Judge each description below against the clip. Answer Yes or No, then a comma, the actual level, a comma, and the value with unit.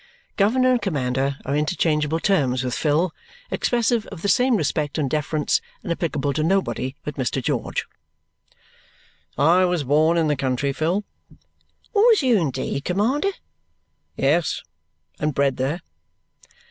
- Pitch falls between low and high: Yes, medium, 155 Hz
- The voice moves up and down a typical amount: No, wide, 5.8 semitones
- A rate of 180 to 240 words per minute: No, slow, 135 wpm